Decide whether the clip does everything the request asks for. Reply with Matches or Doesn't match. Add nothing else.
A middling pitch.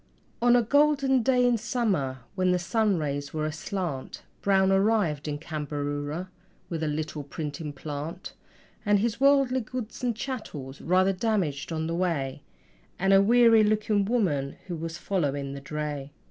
Matches